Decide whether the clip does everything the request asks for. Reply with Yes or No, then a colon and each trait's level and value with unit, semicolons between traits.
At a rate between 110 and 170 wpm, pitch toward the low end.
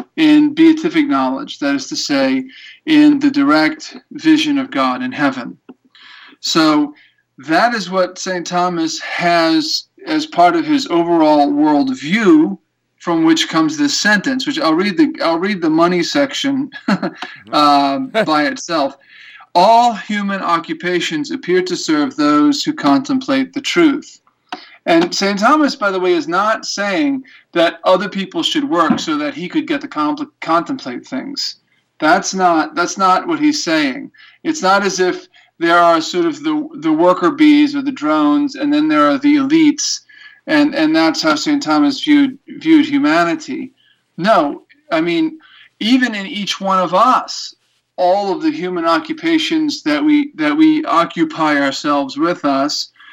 No: average, 155 wpm; very high, 280 Hz